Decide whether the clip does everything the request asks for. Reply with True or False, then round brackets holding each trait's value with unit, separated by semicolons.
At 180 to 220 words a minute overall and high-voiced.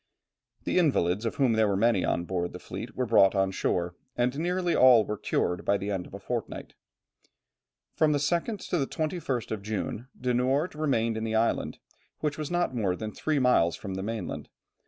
False (200 wpm; 115 Hz)